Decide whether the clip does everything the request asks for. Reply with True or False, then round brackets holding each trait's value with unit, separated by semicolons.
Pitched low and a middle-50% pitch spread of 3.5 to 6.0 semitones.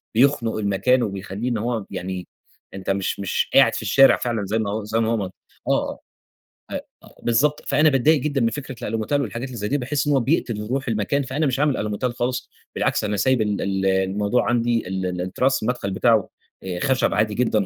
True (115 Hz; 4.4 semitones)